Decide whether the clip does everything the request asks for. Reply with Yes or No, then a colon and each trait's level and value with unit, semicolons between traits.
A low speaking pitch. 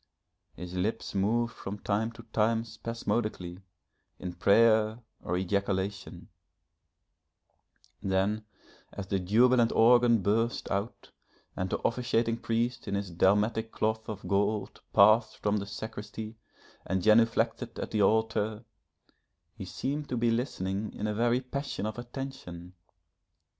Yes: low, 110 Hz